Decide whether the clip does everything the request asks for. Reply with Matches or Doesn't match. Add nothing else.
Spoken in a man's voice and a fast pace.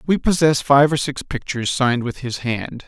Matches